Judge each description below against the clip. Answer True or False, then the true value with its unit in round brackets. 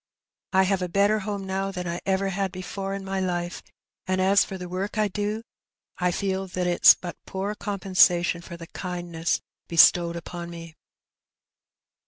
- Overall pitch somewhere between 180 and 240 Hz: True (185 Hz)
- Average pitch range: False (2.0 semitones)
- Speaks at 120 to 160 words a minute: False (170 wpm)